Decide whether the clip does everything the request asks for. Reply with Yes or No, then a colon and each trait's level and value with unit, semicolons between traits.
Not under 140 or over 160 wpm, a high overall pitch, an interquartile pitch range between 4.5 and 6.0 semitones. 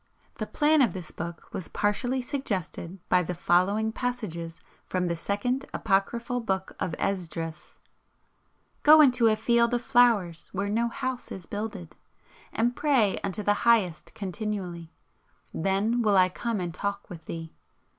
Yes: average, 145 wpm; high, 205 Hz; average, 4.8 semitones